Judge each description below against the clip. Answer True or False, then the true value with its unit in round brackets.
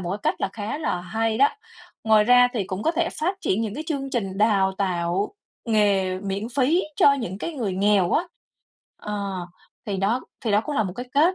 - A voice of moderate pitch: False (215 Hz)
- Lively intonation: False (4.8 semitones)